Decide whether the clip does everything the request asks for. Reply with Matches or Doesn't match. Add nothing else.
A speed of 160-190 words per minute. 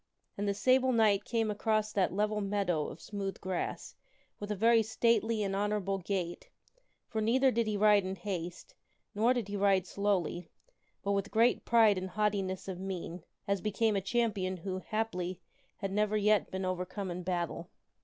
Matches